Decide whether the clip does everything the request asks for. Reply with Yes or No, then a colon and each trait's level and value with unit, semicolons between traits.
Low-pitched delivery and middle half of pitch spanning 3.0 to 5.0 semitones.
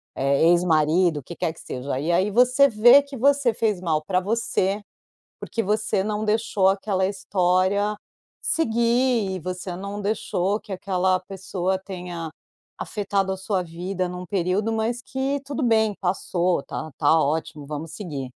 No: high, 190 Hz; average, 3.6 semitones